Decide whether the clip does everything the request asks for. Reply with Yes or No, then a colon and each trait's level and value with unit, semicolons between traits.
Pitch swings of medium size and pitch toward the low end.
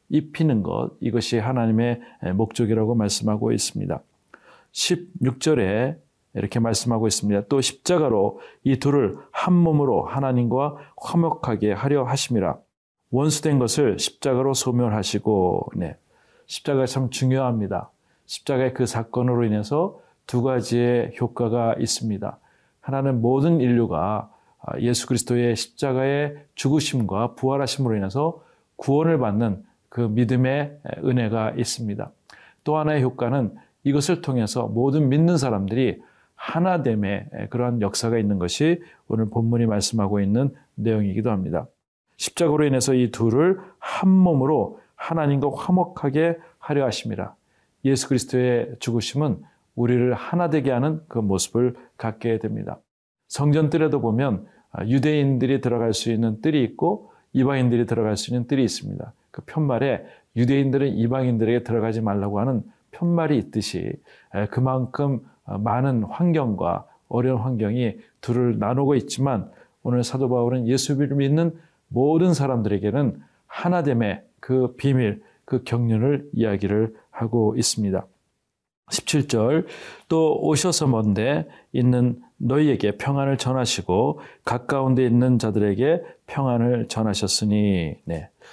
Yes: average, 3.8 semitones; low, 125 Hz